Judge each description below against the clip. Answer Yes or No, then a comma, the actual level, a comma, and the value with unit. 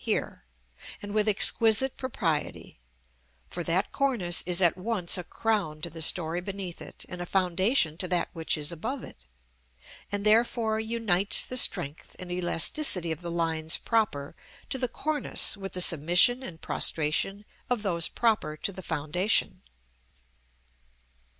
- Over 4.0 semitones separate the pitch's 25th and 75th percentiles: Yes, average, 4.7 semitones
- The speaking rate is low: No, average, 145 wpm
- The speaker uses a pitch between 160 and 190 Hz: Yes, medium, 185 Hz